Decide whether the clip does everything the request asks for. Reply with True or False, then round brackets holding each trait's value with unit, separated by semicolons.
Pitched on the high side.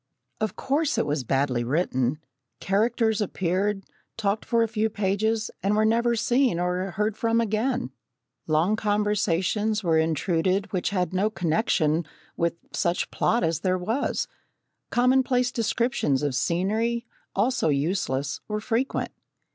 True (205 Hz)